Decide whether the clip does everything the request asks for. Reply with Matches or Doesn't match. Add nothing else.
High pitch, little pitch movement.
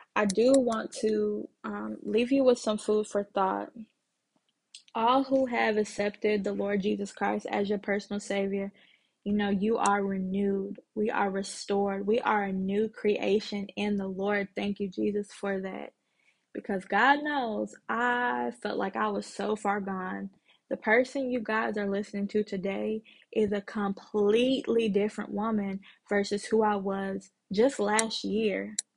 Matches